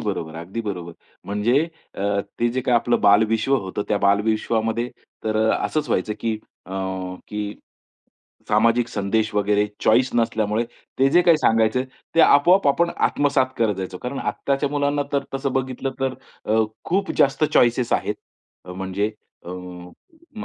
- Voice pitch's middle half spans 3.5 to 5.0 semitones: Yes, average, 4.4 semitones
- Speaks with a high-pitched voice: No, low, 115 Hz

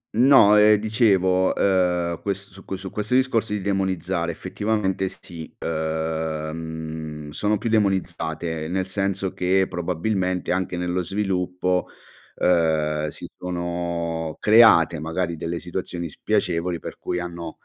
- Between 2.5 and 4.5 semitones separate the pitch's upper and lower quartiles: Yes, average, 2.9 semitones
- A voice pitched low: Yes, very low, 90 Hz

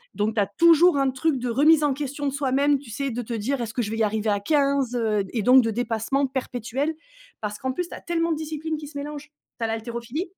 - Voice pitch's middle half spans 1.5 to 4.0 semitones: No, average, 4.5 semitones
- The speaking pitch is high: Yes, very high, 265 Hz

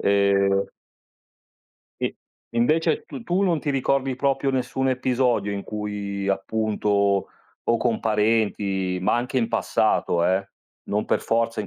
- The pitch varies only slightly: No, average, 4.6 semitones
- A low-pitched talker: Yes, low, 110 Hz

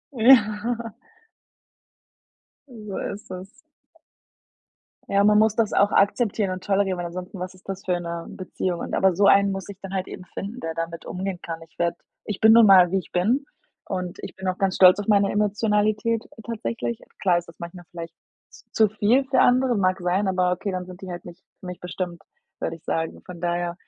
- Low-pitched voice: No, high, 190 Hz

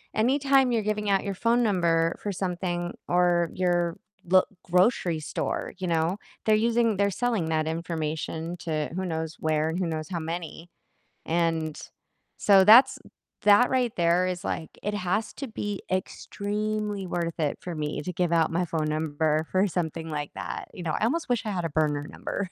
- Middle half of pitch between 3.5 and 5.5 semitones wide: Yes, average, 4.2 semitones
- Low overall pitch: No, medium, 175 Hz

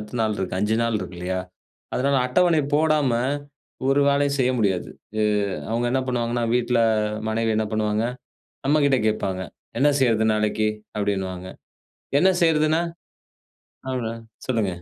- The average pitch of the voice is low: Yes, low, 115 Hz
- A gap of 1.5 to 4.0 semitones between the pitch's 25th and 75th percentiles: No, average, 4.5 semitones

